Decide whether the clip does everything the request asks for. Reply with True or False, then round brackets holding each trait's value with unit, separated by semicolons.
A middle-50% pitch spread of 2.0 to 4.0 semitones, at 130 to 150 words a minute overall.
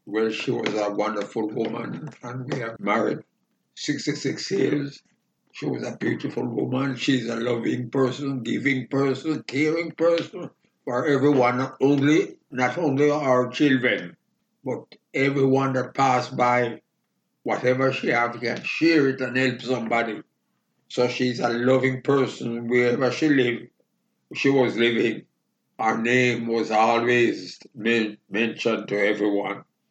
True (2.7 semitones; 140 wpm)